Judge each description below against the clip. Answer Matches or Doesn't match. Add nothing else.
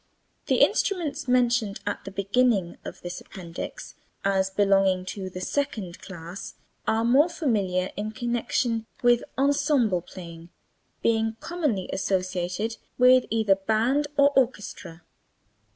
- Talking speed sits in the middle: Doesn't match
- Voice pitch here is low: Doesn't match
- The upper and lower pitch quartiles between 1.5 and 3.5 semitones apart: Doesn't match